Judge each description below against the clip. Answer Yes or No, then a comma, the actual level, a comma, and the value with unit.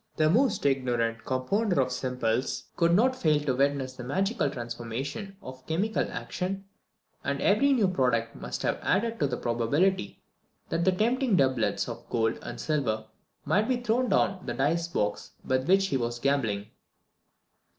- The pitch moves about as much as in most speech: No, wide, 7.8 semitones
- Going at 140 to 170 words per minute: Yes, average, 160 wpm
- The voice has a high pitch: No, medium, 140 Hz